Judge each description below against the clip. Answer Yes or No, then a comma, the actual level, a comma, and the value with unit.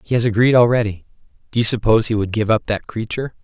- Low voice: Yes, low, 110 Hz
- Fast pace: Yes, fast, 225 wpm